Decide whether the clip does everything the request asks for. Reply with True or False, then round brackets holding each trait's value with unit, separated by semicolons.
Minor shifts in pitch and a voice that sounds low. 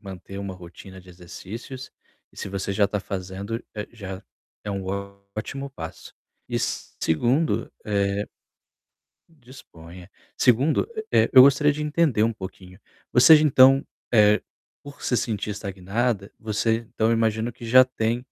False (4.4 semitones; 110 Hz)